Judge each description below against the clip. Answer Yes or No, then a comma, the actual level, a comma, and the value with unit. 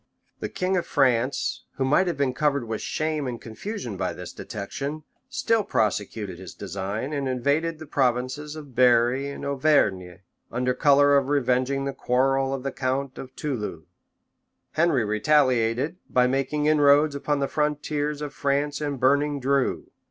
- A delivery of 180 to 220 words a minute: No, average, 155 wpm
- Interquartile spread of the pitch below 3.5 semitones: Yes, average, 2.9 semitones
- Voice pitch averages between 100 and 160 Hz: Yes, medium, 140 Hz